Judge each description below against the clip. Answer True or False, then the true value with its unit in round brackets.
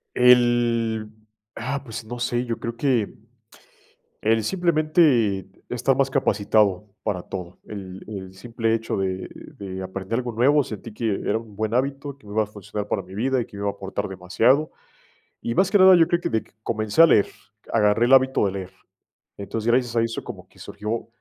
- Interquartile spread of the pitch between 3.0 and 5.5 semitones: True (3.7 semitones)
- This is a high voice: False (115 Hz)